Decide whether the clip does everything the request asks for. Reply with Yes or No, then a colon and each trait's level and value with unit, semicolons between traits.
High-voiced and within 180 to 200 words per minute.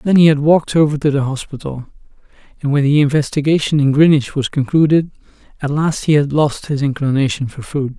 No: medium, 145 Hz; average, 190 wpm